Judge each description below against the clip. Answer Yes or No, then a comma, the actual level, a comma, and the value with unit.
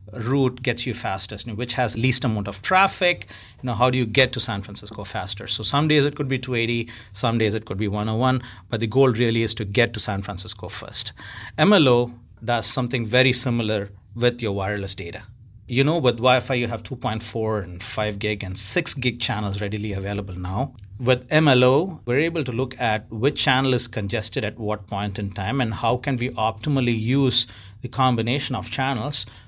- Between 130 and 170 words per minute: No, average, 195 wpm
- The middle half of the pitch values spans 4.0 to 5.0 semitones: No, average, 3.5 semitones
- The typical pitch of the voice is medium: No, low, 115 Hz